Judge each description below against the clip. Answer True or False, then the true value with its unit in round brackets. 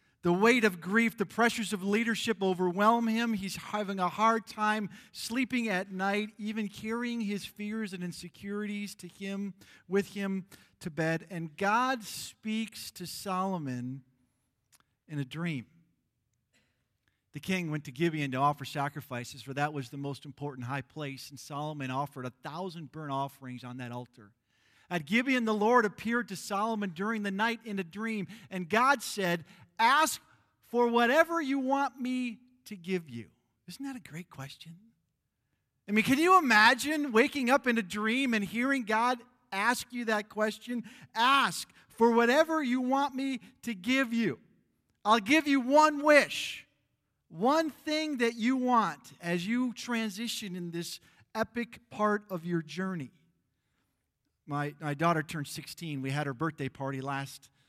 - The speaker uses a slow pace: False (155 wpm)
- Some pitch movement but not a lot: False (7.0 semitones)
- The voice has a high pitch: True (200 Hz)